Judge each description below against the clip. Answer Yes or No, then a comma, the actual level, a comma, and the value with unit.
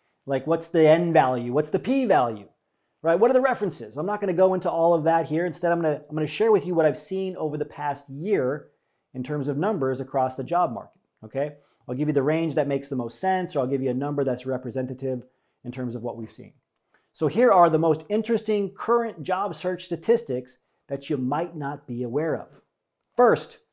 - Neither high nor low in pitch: Yes, medium, 155 Hz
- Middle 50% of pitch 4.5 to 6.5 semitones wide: Yes, average, 5.2 semitones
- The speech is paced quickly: Yes, fast, 235 wpm